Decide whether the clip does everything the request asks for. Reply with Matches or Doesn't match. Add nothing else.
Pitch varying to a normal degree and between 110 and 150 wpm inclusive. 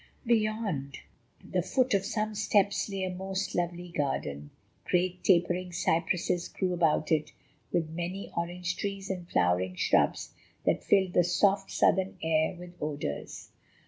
Matches